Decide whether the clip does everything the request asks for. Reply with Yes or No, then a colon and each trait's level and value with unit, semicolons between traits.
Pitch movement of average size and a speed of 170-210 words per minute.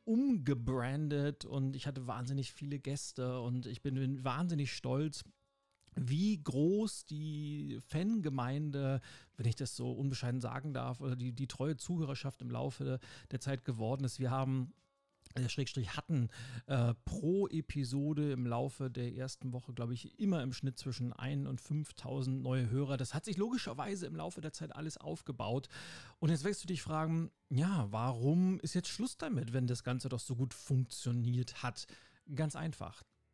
No: average, 3.4 semitones; average, 160 wpm